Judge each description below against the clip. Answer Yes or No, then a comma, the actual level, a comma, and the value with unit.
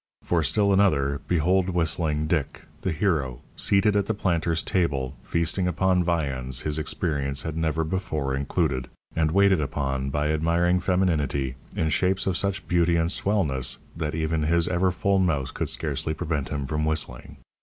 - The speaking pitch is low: Yes, very low, 80 Hz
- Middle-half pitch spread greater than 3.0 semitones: Yes, average, 3.8 semitones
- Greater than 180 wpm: No, average, 160 wpm